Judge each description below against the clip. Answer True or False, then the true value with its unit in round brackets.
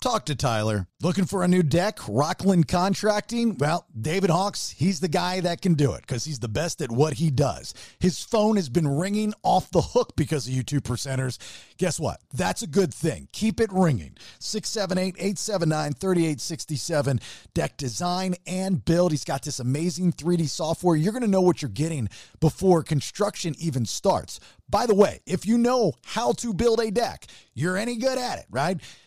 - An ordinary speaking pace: True (185 wpm)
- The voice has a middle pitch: True (175 Hz)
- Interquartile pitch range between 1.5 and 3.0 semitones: False (4.8 semitones)